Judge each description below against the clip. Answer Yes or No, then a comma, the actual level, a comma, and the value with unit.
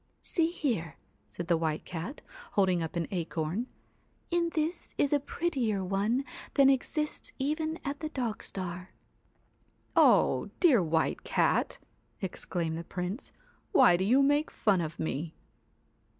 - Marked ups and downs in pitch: Yes, wide, 8.9 semitones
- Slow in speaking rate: No, average, 145 wpm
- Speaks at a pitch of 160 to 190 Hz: No, high, 205 Hz